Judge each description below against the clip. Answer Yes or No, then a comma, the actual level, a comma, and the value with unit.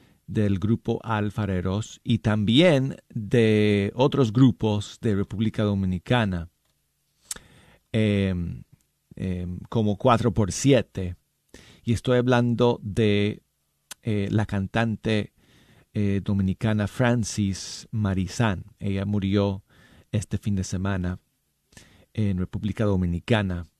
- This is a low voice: Yes, low, 105 Hz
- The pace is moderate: No, slow, 95 wpm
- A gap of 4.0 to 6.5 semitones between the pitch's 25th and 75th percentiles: No, average, 2.8 semitones